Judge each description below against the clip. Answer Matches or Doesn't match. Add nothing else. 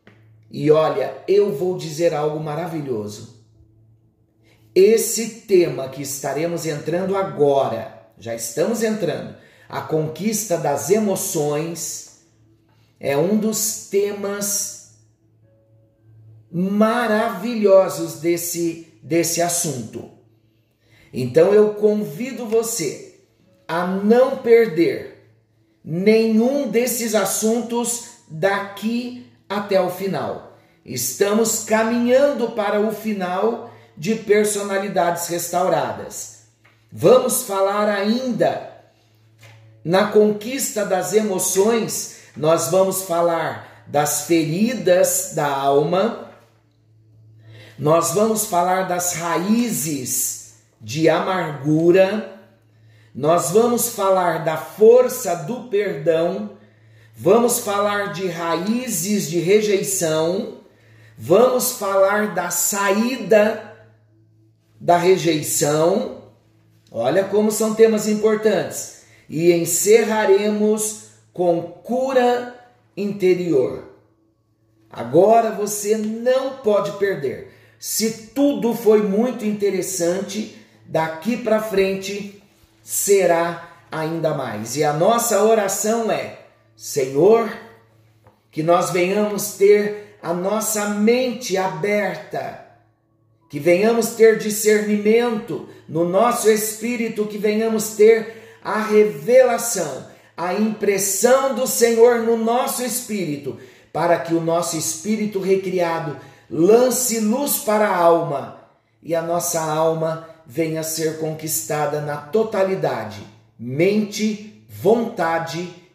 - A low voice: Doesn't match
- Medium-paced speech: Doesn't match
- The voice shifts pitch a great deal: Matches